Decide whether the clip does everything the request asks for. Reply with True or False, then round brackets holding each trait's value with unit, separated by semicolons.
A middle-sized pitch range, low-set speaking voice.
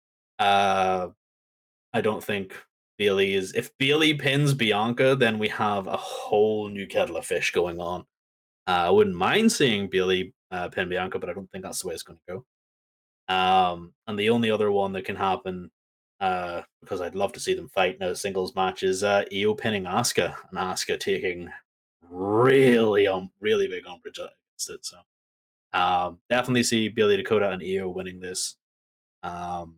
False (7.3 semitones; 100 Hz)